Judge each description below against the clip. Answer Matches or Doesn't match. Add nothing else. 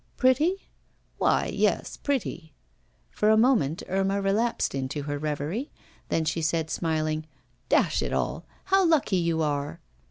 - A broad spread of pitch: Matches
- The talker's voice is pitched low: Doesn't match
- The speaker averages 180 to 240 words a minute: Doesn't match